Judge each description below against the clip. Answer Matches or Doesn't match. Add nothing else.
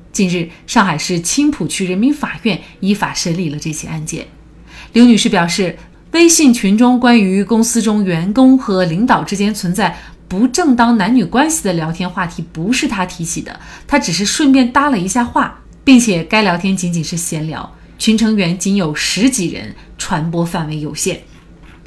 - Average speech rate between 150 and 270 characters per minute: Matches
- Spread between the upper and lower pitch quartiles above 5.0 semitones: Matches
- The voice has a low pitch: Doesn't match